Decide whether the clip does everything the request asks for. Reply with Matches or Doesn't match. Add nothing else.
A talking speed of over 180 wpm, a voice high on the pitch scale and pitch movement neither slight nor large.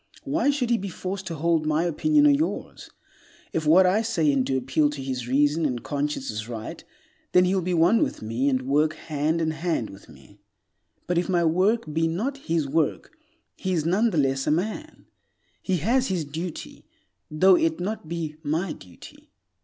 Doesn't match